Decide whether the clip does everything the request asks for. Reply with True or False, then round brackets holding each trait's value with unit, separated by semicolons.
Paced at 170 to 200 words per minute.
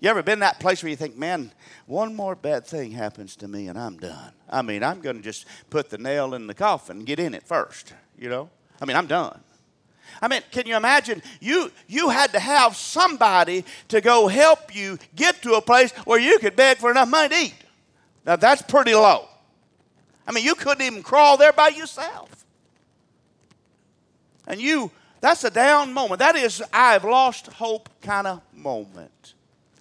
True (195 wpm)